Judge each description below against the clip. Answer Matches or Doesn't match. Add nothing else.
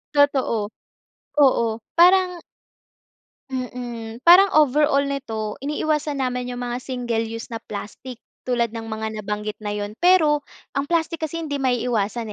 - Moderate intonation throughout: Matches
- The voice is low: Doesn't match